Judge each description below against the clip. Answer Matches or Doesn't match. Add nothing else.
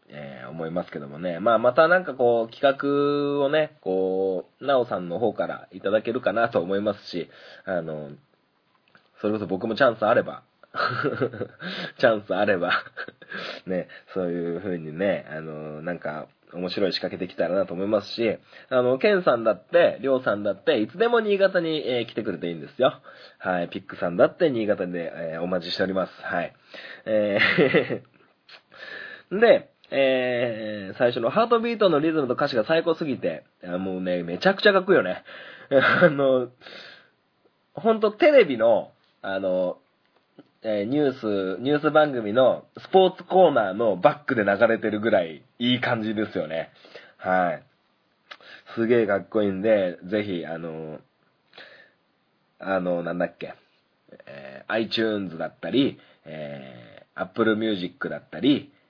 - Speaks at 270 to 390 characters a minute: Matches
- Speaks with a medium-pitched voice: Doesn't match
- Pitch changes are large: Matches